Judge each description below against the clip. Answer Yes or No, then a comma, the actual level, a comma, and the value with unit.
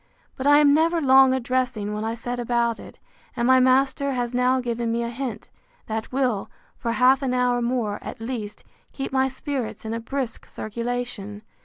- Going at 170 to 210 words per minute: Yes, average, 190 wpm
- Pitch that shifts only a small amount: Yes, narrow, 2.3 semitones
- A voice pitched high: Yes, high, 245 Hz